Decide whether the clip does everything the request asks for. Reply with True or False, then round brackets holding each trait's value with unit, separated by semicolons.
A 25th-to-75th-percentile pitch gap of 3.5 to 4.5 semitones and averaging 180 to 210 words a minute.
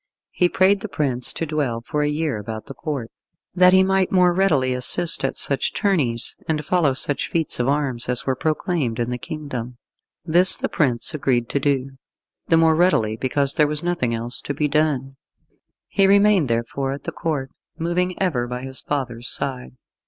False (5.2 semitones; 190 wpm)